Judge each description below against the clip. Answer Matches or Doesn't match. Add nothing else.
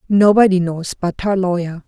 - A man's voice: Doesn't match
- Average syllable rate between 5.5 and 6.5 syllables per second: Doesn't match